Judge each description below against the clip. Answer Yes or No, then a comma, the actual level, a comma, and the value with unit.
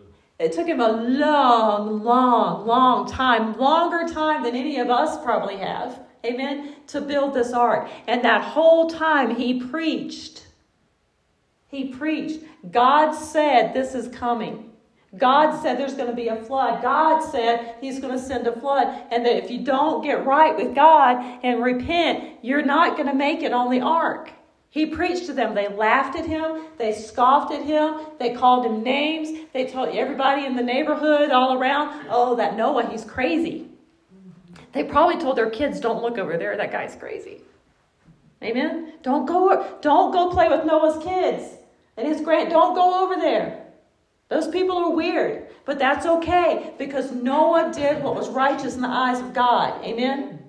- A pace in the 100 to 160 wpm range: No, average, 175 wpm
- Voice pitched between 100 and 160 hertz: No, very high, 275 Hz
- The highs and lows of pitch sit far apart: No, average, 4.3 semitones